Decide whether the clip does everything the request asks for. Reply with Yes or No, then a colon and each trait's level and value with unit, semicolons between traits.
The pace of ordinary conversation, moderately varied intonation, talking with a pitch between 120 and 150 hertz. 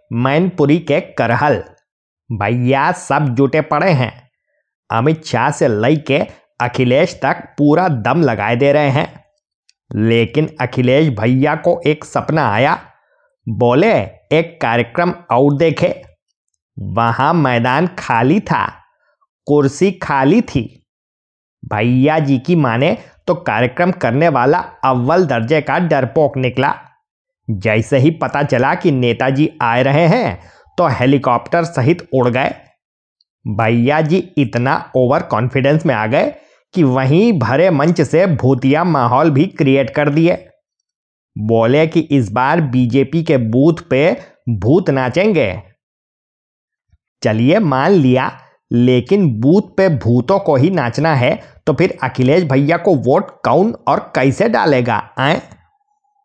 Yes: average, 125 wpm; average, 4.8 semitones; medium, 140 Hz